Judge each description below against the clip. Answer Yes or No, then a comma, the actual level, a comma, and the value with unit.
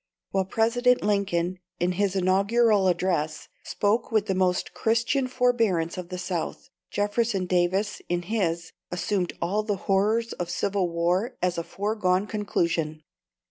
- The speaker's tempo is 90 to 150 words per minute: Yes, average, 140 wpm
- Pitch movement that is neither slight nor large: Yes, average, 3.3 semitones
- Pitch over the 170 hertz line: Yes, high, 190 Hz